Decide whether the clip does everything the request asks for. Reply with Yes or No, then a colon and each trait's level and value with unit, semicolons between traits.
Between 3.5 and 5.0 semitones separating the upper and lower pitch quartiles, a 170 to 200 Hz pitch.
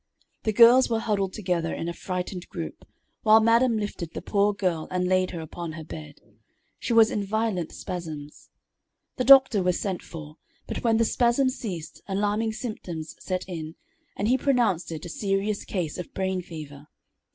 Yes: average, 4.7 semitones; high, 190 Hz